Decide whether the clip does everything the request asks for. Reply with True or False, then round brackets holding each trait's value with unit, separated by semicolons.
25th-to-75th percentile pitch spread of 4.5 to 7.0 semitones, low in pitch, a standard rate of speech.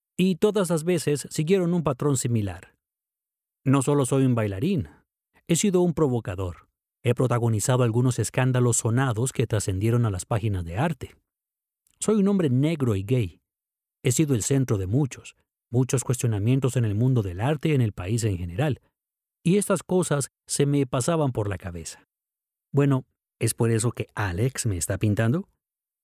True (4.8 semitones; 130 Hz; 165 wpm)